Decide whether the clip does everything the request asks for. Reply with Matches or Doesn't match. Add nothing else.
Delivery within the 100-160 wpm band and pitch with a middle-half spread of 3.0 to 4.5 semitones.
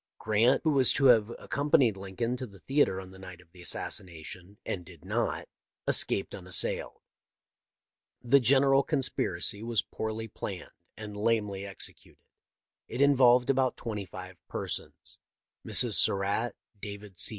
Doesn't match